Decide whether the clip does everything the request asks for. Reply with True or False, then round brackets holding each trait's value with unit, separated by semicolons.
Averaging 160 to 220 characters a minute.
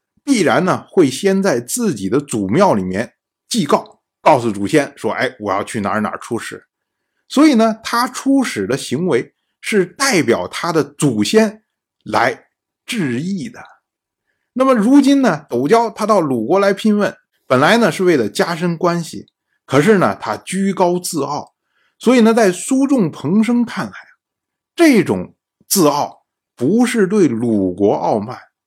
True (215 characters per minute)